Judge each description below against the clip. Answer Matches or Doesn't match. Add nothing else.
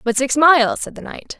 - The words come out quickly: Matches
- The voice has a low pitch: Doesn't match